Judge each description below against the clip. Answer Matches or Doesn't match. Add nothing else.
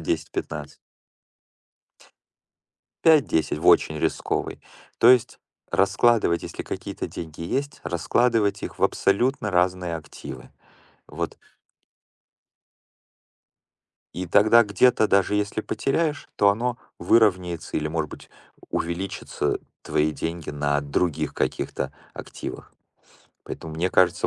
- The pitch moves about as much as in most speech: Doesn't match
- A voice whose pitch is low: Matches